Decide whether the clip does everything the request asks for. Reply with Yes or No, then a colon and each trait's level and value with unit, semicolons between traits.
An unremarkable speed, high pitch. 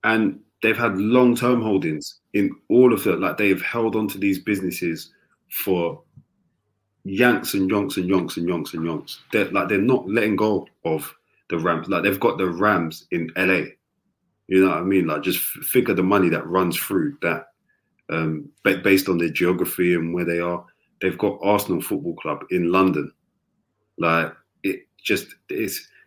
No: average, 175 wpm; very low, 95 Hz